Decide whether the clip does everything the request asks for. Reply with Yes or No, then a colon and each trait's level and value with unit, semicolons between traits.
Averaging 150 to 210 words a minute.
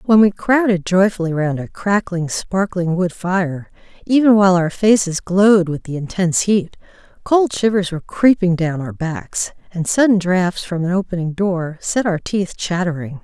Yes: average, 170 wpm